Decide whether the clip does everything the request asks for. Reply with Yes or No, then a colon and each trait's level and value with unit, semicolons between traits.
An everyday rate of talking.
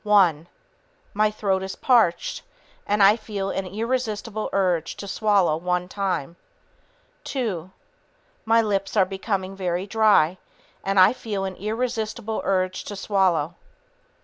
No: slow, 125 wpm